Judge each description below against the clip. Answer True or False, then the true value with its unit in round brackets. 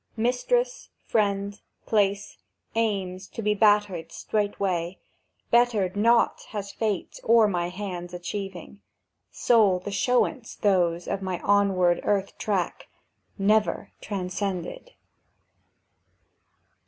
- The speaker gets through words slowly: True (95 wpm)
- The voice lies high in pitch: True (200 Hz)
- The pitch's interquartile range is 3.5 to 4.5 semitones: False (2.8 semitones)